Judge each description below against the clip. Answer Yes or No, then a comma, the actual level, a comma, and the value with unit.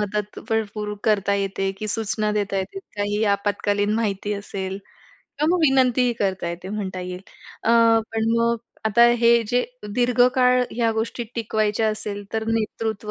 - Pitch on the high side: Yes, high, 215 Hz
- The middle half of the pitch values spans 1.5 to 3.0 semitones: Yes, narrow, 2.4 semitones